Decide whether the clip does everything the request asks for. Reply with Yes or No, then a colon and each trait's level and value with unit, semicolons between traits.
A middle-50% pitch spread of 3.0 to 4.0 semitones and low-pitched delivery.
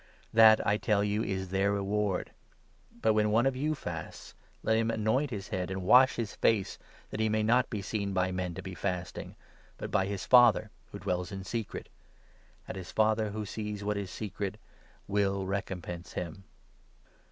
No: narrow, 2.4 semitones; low, 100 Hz